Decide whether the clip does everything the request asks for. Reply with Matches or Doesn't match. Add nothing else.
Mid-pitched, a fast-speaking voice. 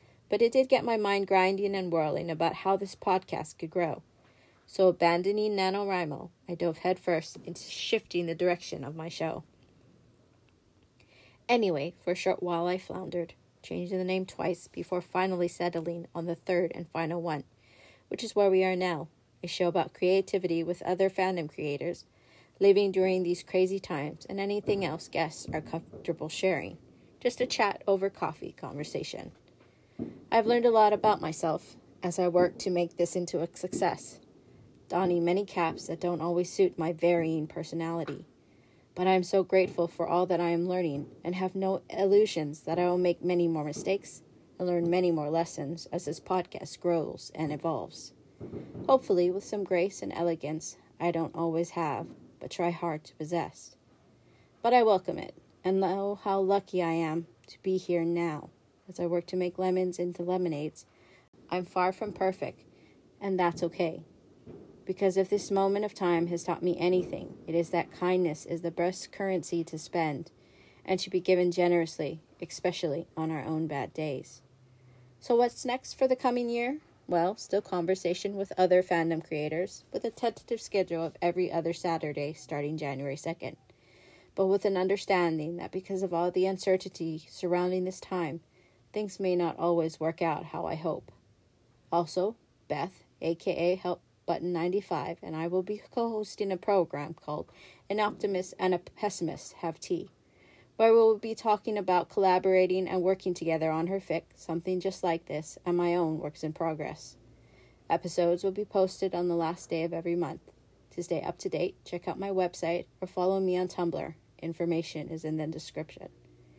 Doesn't match